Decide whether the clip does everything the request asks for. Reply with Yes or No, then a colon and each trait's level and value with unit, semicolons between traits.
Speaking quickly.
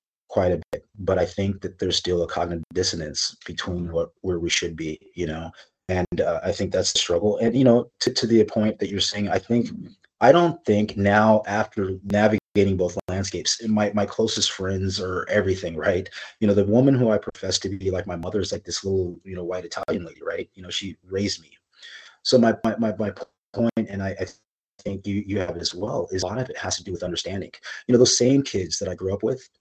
Yes: fast, 235 wpm